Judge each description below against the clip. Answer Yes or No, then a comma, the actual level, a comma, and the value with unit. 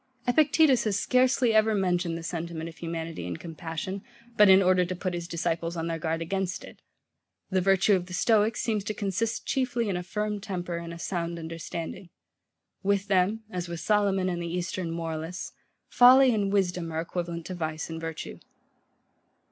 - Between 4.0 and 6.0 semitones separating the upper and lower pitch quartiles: No, average, 3.4 semitones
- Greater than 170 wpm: Yes, average, 180 wpm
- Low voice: No, medium, 180 Hz